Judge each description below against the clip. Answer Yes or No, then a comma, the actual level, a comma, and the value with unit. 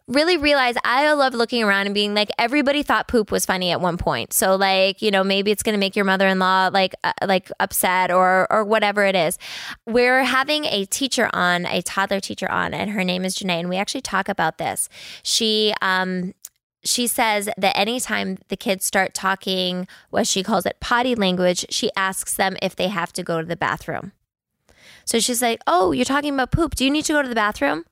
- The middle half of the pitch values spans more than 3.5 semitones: Yes, average, 4.2 semitones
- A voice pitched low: No, high, 200 Hz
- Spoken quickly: Yes, fast, 215 wpm